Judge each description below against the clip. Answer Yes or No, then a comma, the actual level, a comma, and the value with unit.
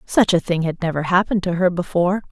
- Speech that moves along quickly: Yes, fast, 235 wpm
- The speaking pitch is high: No, medium, 180 Hz